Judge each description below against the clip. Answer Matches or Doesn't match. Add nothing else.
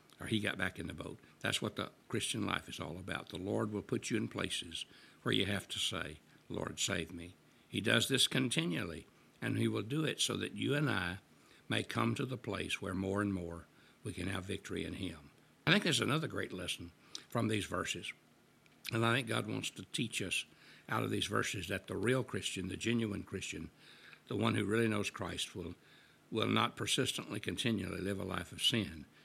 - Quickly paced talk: Matches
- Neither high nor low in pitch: Doesn't match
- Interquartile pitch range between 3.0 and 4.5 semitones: Matches